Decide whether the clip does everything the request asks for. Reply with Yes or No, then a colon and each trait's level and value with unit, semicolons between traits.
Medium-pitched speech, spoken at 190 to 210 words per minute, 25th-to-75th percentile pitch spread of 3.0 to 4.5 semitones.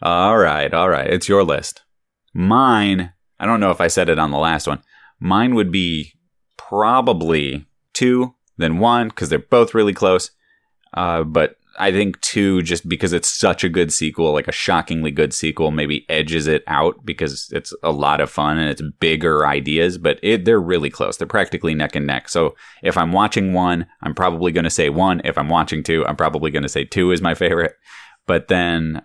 No: very low, 85 Hz; average, 200 wpm; average, 3.7 semitones